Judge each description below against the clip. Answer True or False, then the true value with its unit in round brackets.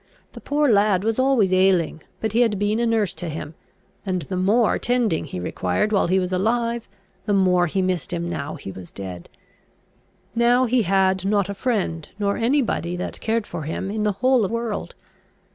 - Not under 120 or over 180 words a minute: False (195 wpm)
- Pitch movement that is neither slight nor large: True (4.2 semitones)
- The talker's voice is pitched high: True (200 Hz)